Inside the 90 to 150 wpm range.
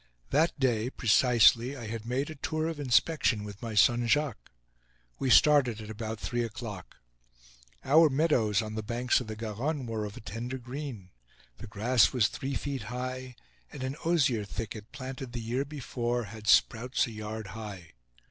No: average, 170 wpm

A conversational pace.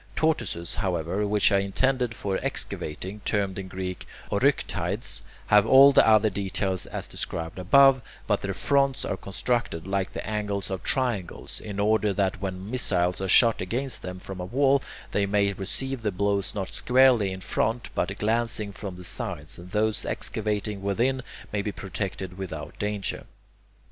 Yes: average, 165 wpm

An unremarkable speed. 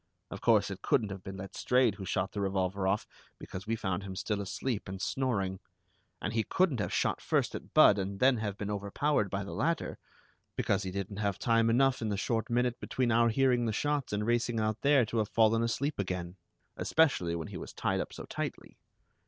No: fast, 210 wpm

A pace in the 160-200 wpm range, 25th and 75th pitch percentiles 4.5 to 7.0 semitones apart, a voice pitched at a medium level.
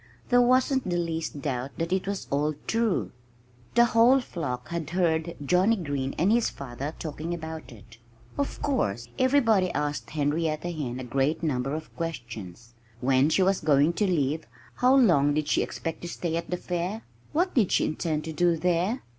Yes: average, 180 wpm; average, 4.8 semitones; medium, 165 Hz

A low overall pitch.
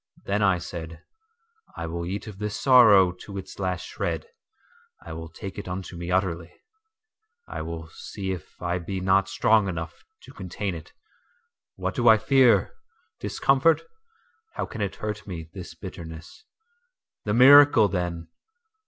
Yes: low, 100 Hz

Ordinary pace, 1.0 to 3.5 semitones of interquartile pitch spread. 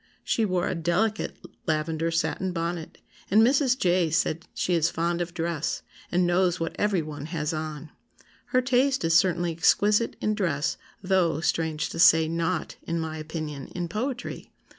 Yes: average, 160 wpm; average, 2.8 semitones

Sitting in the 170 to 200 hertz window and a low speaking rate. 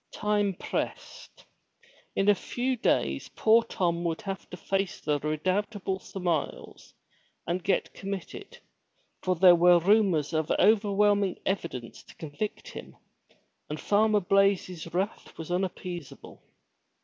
Yes: high, 190 Hz; slow, 125 wpm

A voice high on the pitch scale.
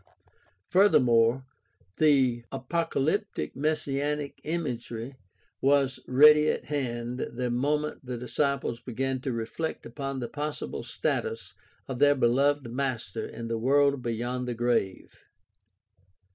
No: low, 135 Hz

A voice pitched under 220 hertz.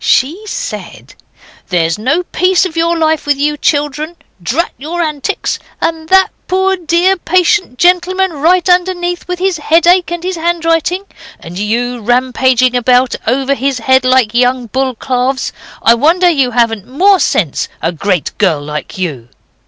No: very high, 290 Hz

